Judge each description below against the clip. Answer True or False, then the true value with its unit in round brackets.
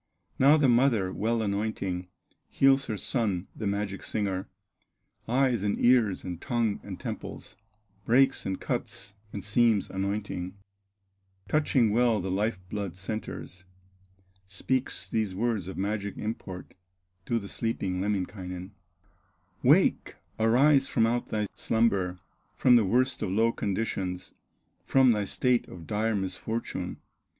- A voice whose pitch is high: False (105 Hz)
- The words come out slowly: True (125 wpm)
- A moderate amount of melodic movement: True (3.6 semitones)